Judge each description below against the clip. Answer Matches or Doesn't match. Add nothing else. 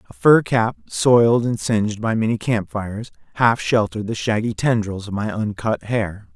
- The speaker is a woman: Doesn't match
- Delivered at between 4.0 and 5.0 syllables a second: Matches